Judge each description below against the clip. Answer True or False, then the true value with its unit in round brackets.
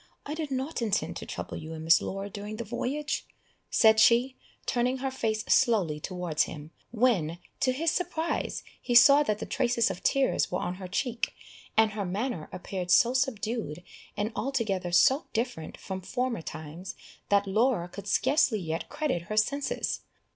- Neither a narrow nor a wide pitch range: False (6.1 semitones)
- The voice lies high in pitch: True (220 Hz)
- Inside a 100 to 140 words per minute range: False (170 wpm)